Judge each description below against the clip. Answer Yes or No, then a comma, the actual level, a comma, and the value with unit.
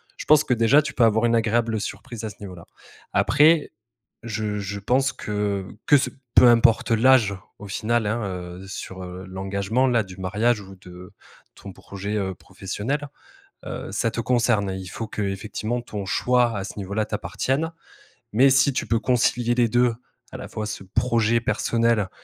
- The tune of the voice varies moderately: Yes, average, 3.5 semitones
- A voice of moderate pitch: No, low, 110 Hz